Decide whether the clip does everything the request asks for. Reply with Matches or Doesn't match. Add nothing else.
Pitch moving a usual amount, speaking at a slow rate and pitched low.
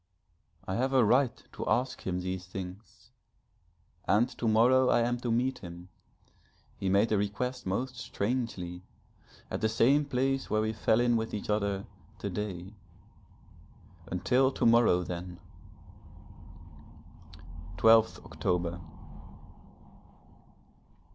Matches